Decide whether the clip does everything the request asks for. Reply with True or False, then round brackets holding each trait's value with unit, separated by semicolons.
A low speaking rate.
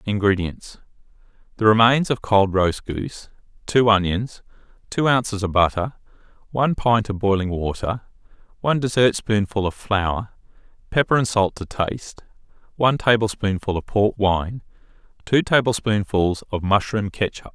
True (125 wpm)